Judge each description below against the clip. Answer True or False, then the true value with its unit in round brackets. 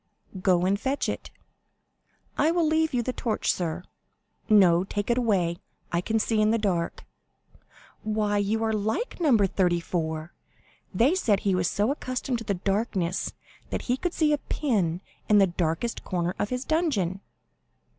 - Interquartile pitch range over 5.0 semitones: True (5.4 semitones)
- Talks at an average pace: True (160 wpm)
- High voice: True (210 Hz)